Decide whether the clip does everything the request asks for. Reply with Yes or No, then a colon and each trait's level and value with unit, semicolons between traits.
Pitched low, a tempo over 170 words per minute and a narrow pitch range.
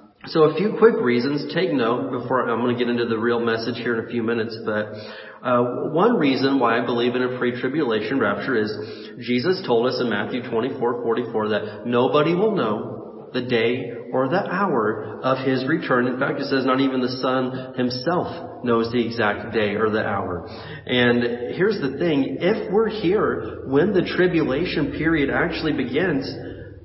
Yes: low, 125 Hz; average, 180 wpm; narrow, 2.2 semitones